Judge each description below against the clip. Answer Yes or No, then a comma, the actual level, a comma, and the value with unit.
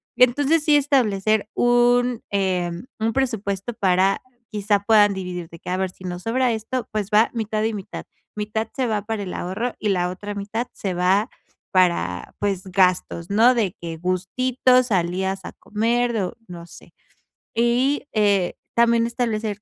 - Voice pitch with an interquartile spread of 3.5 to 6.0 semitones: Yes, average, 4.1 semitones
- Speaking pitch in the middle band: No, high, 210 Hz